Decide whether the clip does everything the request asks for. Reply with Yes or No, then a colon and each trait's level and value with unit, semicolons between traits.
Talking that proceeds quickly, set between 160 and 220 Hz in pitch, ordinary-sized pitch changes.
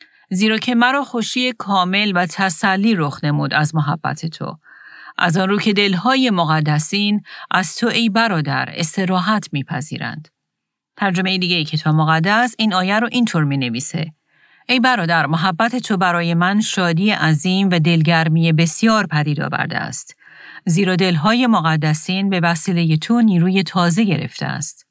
No: average, 145 wpm; medium, 185 Hz; average, 4.9 semitones